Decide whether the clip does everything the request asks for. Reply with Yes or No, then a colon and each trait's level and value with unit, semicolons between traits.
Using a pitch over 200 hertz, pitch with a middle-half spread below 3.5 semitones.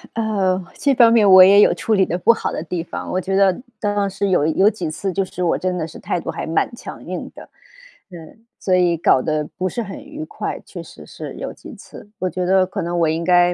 No: medium, 185 Hz; average, 2.8 semitones